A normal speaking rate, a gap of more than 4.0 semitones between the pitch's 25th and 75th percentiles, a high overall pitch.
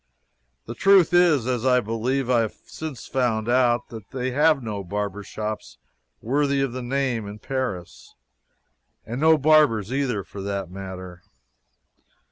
No: average, 145 wpm; average, 4.6 semitones; low, 120 Hz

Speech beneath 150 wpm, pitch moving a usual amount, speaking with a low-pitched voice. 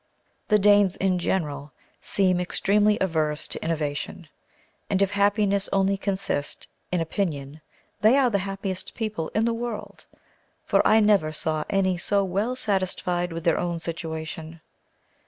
No: average, 140 wpm; average, 3.8 semitones; high, 190 Hz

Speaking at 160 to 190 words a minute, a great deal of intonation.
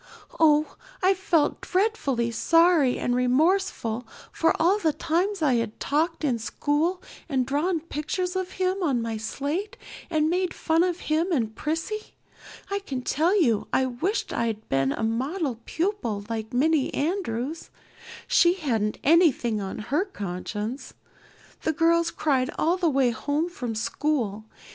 No: average, 145 wpm; wide, 6.6 semitones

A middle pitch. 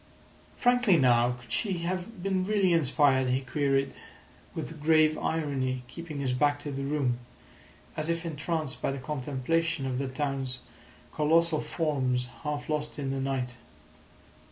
Yes: medium, 145 Hz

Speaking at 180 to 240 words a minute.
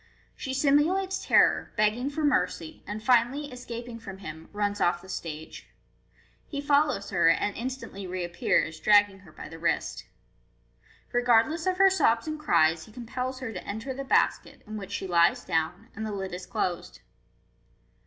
No: average, 165 wpm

